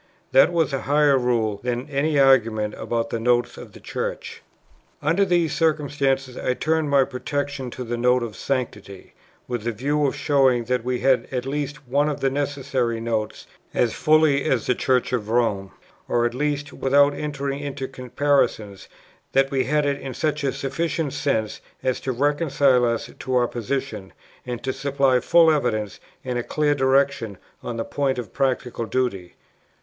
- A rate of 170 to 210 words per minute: Yes, average, 175 wpm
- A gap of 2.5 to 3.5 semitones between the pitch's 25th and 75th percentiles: Yes, average, 2.9 semitones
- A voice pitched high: No, low, 135 Hz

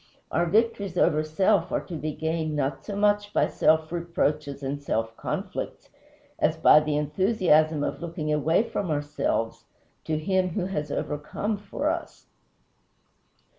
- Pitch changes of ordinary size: Yes, average, 3.9 semitones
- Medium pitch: Yes, medium, 160 Hz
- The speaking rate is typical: Yes, average, 145 wpm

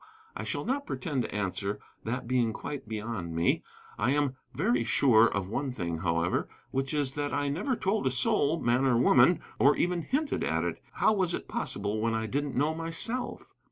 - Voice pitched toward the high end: No, low, 130 Hz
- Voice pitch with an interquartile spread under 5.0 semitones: No, wide, 5.5 semitones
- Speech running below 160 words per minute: No, average, 190 wpm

